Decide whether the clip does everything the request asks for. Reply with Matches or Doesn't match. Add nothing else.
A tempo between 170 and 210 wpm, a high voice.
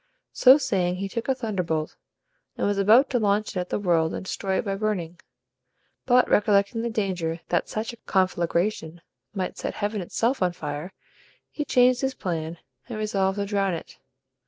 Matches